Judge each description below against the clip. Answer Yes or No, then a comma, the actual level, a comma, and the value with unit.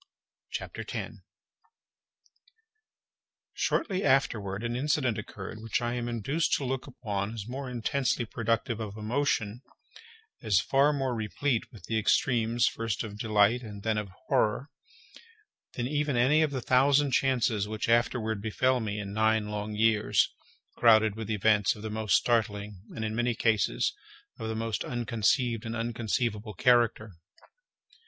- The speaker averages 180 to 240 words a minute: No, average, 145 wpm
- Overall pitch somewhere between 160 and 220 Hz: No, low, 115 Hz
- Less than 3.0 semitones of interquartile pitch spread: Yes, narrow, 2.6 semitones